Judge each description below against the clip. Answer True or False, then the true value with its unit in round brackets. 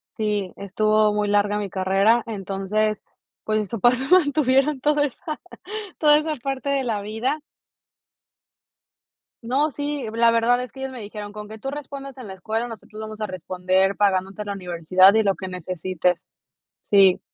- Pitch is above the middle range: True (215 Hz)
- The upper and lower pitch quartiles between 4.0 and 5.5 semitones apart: True (4.9 semitones)